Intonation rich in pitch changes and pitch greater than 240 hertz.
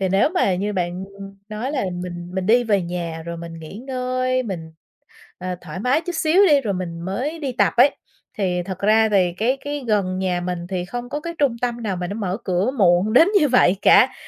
No: wide, 6.0 semitones; high, 200 Hz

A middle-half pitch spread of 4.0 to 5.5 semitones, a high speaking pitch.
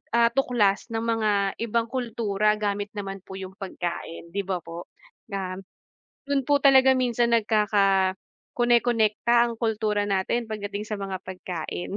No: average, 3.2 semitones; high, 210 Hz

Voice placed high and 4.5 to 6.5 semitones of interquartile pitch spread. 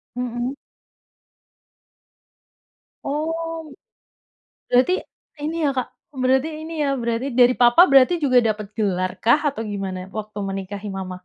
Yes: high, 245 Hz; wide, 5.4 semitones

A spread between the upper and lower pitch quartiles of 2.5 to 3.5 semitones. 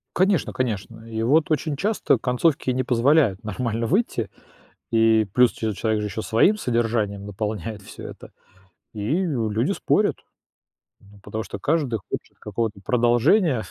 No: average, 4.2 semitones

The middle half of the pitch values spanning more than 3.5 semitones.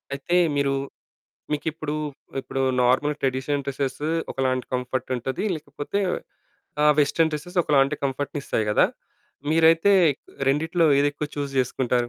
No: narrow, 2.5 semitones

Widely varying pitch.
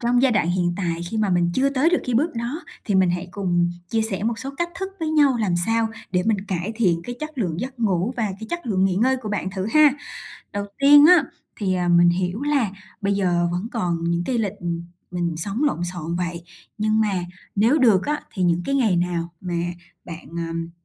Yes: wide, 5.8 semitones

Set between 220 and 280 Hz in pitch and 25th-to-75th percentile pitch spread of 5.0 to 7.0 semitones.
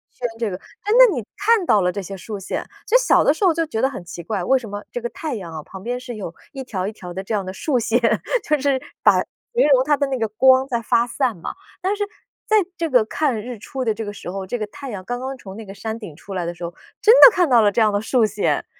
Yes: high, 235 Hz; wide, 5.6 semitones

